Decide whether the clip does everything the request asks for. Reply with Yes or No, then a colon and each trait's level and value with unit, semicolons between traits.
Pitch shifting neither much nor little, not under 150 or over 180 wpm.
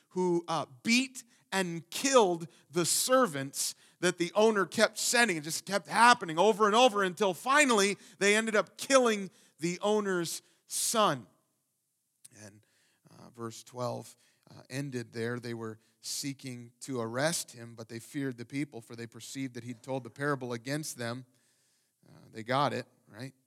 No: wide, 8.4 semitones; average, 155 wpm